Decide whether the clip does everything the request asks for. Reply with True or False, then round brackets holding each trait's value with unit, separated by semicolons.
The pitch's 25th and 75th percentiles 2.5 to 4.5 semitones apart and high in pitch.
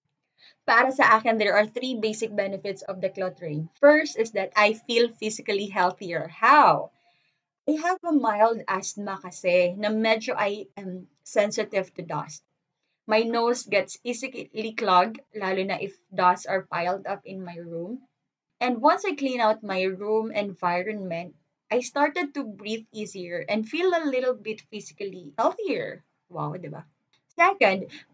True (4.1 semitones; 210 Hz)